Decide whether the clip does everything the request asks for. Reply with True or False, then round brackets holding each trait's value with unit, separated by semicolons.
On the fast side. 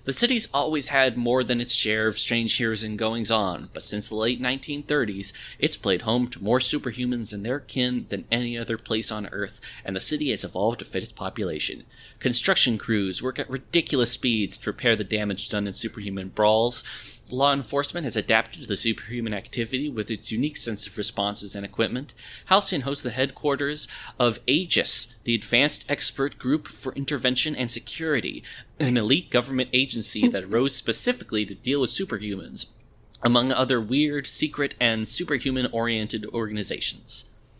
False (170 wpm)